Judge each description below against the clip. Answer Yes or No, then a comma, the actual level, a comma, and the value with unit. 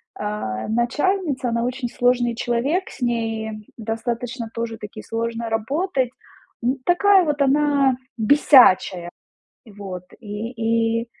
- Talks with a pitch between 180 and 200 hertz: No, high, 235 Hz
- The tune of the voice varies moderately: Yes, average, 3.1 semitones